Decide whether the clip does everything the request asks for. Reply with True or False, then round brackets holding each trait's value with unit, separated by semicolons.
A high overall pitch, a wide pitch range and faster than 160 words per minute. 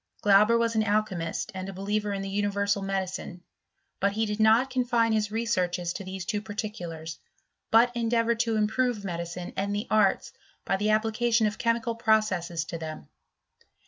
False (210 Hz; 2.9 semitones; 170 wpm)